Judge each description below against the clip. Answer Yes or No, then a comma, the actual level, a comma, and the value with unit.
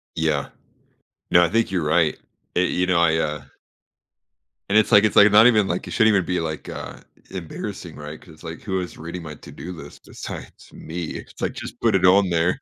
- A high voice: No, very low, 85 Hz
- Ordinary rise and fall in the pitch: Yes, average, 3.1 semitones